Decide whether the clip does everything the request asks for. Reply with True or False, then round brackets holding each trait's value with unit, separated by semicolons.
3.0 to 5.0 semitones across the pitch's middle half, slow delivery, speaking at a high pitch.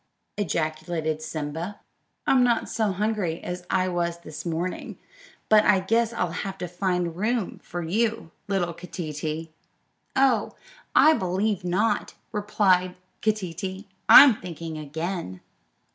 False (4.1 semitones; 120 wpm; 180 Hz)